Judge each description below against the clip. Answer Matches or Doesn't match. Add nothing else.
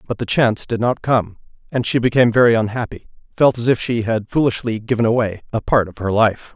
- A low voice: Matches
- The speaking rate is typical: Doesn't match